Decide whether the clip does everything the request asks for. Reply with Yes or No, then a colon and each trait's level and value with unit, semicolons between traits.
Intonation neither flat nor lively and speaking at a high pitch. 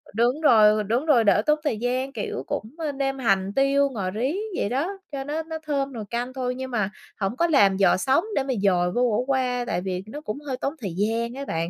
Yes: average, 4.6 semitones; very high, 250 Hz